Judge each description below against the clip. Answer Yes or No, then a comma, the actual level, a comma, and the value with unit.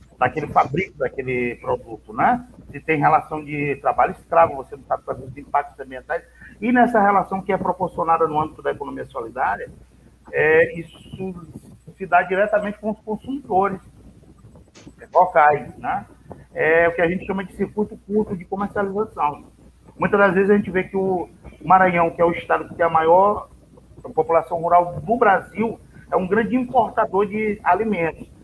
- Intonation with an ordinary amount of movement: Yes, average, 4.3 semitones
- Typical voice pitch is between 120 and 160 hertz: No, medium, 185 Hz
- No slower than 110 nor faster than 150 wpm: No, average, 160 wpm